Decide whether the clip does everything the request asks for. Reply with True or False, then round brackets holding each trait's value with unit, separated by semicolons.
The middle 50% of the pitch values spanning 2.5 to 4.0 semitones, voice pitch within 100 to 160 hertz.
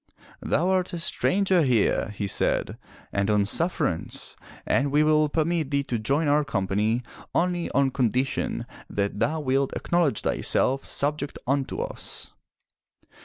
False (5.2 semitones; 140 Hz)